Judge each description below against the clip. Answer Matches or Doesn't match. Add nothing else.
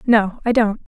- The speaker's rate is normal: Matches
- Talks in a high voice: Matches